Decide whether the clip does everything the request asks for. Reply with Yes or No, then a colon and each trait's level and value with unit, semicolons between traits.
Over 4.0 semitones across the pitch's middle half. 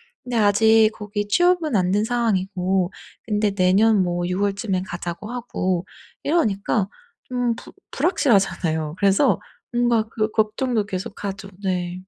No: average, 3.4 semitones